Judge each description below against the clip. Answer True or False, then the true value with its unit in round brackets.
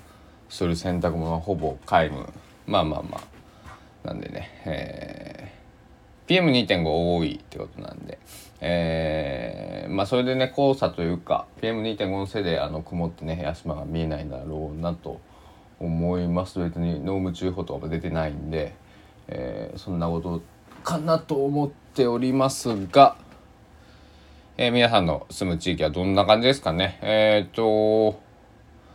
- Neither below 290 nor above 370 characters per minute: False (270 characters per minute)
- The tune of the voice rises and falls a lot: False (5.0 semitones)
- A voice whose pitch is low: True (90 Hz)